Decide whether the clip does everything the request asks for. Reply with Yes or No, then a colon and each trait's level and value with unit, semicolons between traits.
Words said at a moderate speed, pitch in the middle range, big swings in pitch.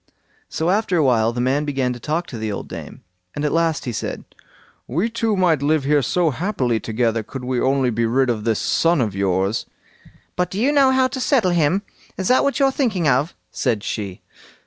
No: fast, 215 wpm; medium, 145 Hz; wide, 7.3 semitones